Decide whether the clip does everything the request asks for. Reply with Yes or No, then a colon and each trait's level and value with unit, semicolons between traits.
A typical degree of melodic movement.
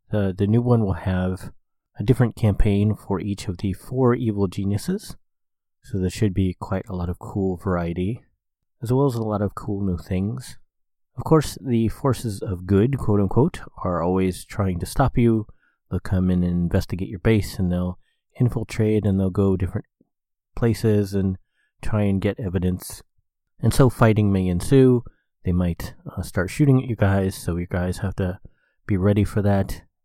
Yes: average, 3.3 semitones